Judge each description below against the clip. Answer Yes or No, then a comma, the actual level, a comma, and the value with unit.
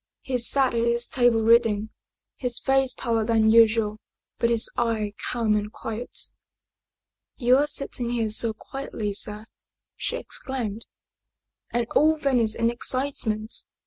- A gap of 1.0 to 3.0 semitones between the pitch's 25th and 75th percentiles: Yes, narrow, 2.5 semitones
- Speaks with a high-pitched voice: Yes, high, 230 Hz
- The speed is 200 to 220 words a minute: No, average, 140 wpm